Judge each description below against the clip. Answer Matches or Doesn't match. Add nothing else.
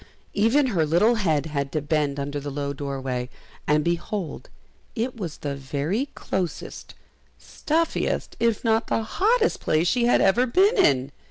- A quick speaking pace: Doesn't match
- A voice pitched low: Doesn't match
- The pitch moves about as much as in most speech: Doesn't match